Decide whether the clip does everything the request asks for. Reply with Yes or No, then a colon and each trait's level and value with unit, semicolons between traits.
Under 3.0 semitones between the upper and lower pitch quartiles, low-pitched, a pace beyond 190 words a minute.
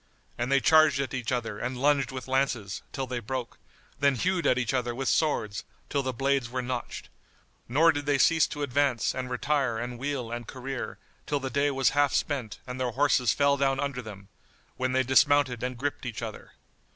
Yes: narrow, 2.5 semitones; low, 130 Hz; average, 200 wpm